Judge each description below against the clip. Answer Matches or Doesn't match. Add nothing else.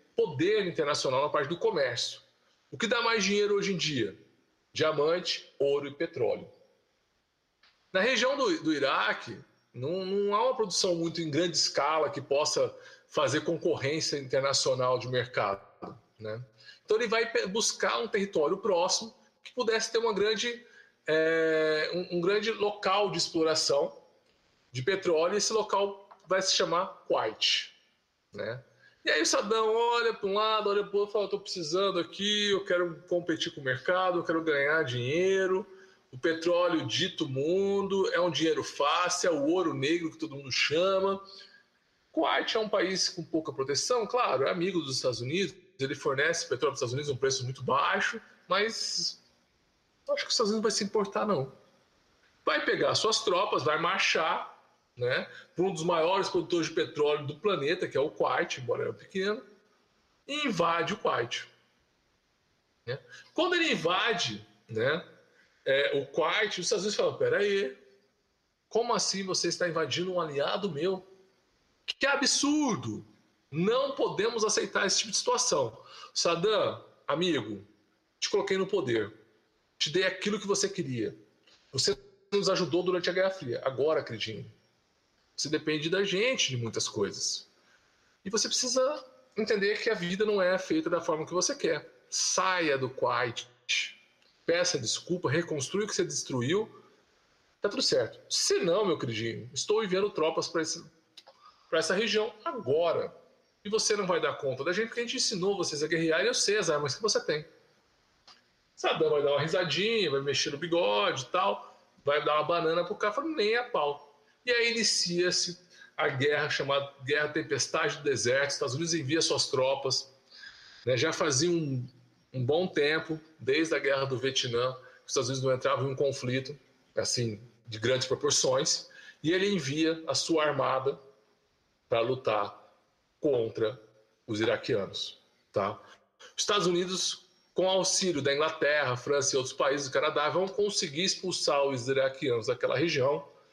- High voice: Doesn't match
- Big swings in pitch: Matches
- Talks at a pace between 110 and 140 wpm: Doesn't match